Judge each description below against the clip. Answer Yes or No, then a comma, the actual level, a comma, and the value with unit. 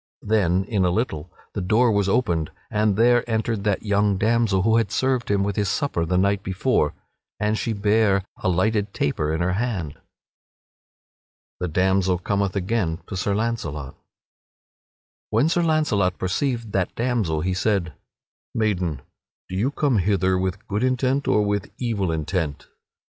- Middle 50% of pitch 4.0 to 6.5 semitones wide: No, average, 3.6 semitones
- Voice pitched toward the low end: Yes, low, 100 Hz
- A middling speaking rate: Yes, average, 160 wpm